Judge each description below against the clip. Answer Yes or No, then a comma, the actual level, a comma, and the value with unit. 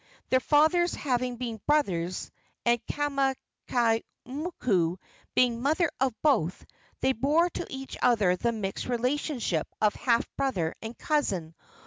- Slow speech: Yes, slow, 125 wpm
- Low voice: No, very high, 250 Hz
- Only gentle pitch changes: No, average, 4.8 semitones